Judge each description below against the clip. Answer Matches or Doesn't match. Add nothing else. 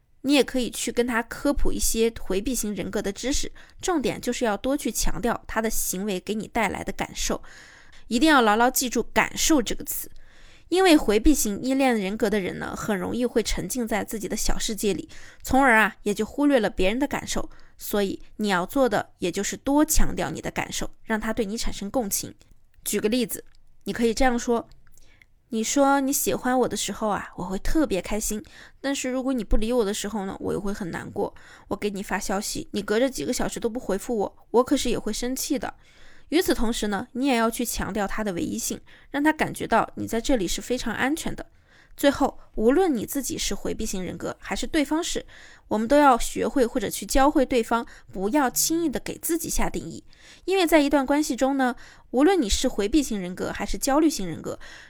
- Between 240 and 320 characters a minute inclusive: Matches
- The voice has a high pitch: Matches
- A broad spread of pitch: Doesn't match